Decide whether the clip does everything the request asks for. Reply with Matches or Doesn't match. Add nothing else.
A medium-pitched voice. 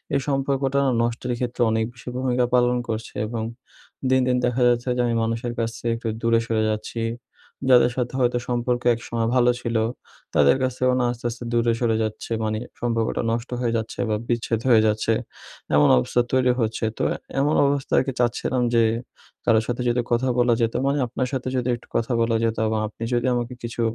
Doesn't match